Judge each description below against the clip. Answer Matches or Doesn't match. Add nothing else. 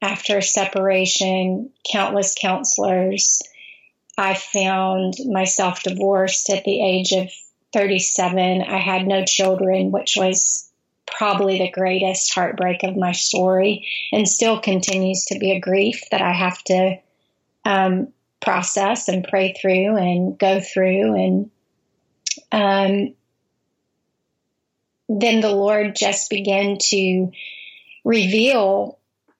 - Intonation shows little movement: Matches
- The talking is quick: Doesn't match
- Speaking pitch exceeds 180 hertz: Matches